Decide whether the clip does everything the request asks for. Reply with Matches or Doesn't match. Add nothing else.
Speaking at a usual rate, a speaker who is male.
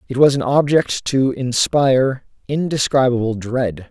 Doesn't match